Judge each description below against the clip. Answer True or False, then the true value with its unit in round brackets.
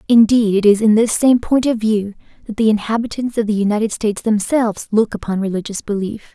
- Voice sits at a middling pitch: False (215 Hz)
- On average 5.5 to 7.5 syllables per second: True (5.9 syllables/s)